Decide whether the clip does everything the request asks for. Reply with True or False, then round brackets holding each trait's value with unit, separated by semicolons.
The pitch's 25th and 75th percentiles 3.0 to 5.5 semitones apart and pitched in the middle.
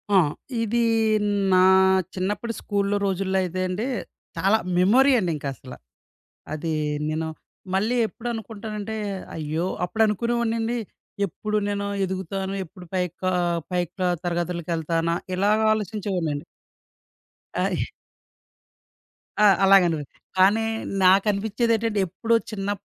False (3.4 semitones; 195 Hz)